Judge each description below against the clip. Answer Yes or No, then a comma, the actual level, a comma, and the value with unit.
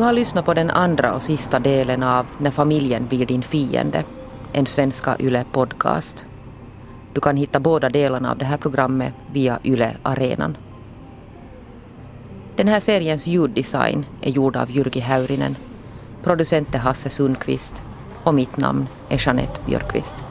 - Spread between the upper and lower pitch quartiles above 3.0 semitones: No, narrow, 2.5 semitones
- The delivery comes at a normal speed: Yes, average, 140 wpm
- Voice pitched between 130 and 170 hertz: Yes, low, 135 Hz